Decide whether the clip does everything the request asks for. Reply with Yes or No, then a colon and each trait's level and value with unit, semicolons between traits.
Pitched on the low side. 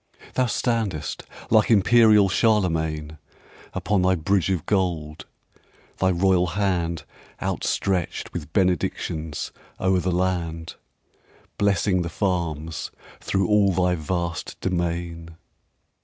Yes: very low, 90 Hz